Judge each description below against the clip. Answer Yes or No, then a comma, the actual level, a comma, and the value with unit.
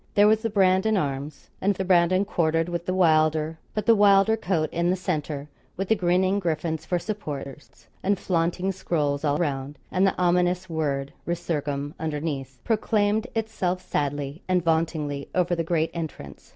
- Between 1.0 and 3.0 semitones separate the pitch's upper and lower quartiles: No, average, 3.9 semitones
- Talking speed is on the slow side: No, average, 165 wpm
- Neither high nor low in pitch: Yes, medium, 170 Hz